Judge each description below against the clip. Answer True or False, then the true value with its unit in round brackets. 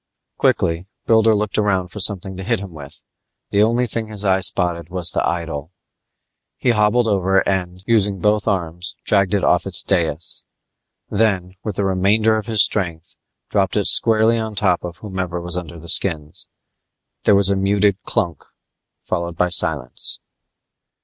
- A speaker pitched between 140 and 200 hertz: False (95 Hz)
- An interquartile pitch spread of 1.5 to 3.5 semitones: True (3.2 semitones)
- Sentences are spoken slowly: False (165 wpm)